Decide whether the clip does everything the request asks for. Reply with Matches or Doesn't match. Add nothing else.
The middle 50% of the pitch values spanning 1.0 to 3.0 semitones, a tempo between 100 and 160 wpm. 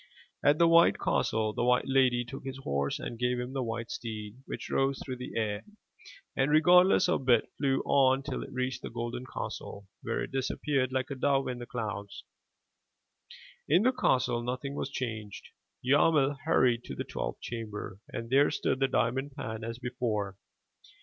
Doesn't match